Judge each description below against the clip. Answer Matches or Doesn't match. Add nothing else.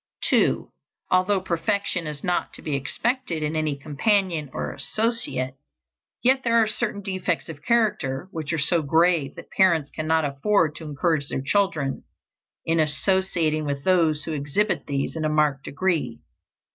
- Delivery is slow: Doesn't match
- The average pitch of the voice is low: Doesn't match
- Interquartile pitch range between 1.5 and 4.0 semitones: Doesn't match